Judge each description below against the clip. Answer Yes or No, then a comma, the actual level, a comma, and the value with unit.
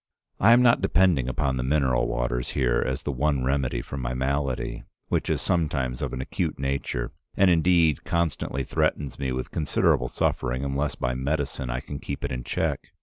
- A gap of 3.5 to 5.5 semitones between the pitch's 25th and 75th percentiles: No, average, 2.9 semitones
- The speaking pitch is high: No, very low, 70 Hz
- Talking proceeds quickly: No, average, 185 wpm